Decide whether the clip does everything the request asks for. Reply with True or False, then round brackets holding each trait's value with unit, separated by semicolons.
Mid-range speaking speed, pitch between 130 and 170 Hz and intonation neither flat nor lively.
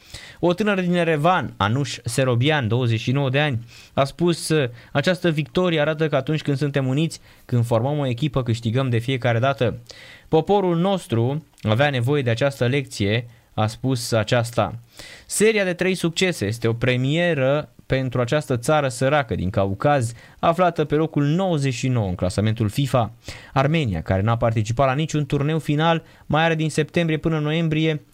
True (150 wpm; 140 Hz; 5.0 semitones)